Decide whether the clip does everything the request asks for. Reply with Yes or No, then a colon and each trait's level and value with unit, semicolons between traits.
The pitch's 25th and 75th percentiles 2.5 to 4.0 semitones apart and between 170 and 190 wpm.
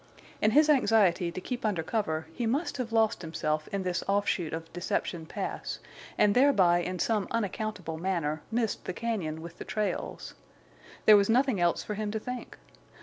No: average, 4.6 semitones; average, 175 wpm